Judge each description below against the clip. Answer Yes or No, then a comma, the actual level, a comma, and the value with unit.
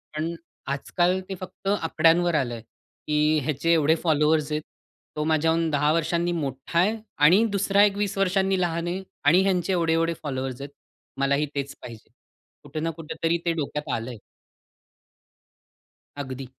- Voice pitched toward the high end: No, medium, 160 Hz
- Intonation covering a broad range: No, average, 3.2 semitones